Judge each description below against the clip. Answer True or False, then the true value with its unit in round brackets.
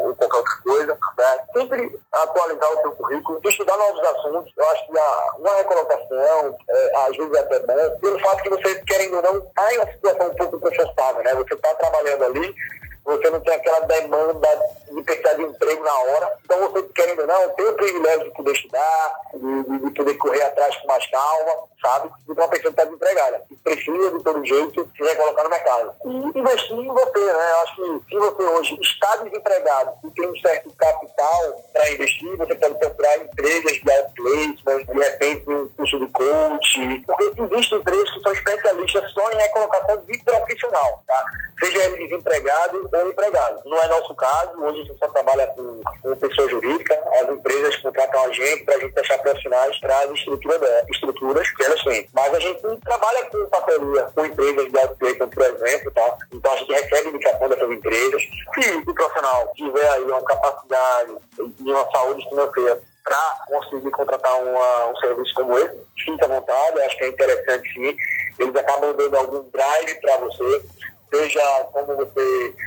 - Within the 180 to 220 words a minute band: True (185 wpm)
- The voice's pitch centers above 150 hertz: True (190 Hz)